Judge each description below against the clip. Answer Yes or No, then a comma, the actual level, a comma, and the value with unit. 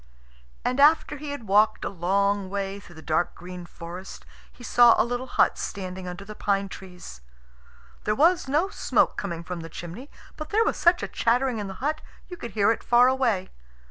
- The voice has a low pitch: No, high, 205 Hz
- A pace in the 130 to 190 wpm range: No, average, 200 wpm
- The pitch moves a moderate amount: No, wide, 6.1 semitones